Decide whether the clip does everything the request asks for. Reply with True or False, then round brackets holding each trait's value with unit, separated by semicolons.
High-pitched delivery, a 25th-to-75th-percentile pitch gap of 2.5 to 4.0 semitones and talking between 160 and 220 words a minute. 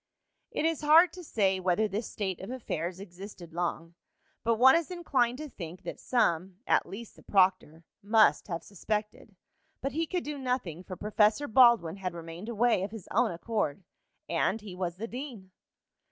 False (210 Hz; 5.2 semitones; 175 wpm)